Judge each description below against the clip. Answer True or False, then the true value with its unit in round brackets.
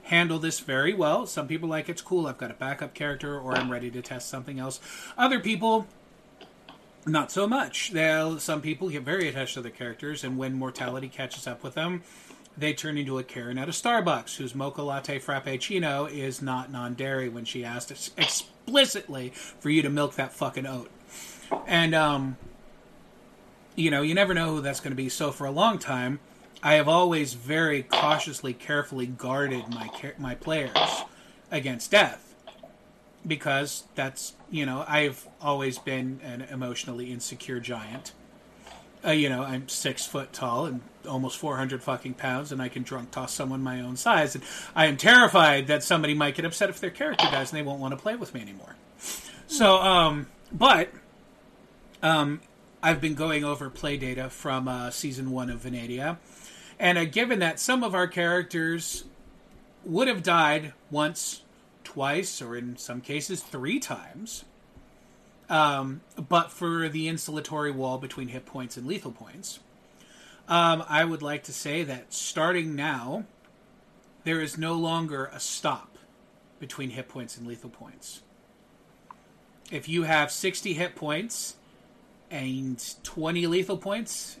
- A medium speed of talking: True (165 wpm)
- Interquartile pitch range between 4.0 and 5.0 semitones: True (4.3 semitones)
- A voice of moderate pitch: True (145 Hz)